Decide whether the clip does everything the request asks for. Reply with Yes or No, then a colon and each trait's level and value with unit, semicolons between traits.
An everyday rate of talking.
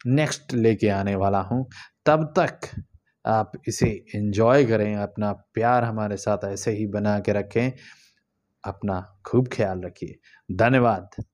Yes: average, 130 wpm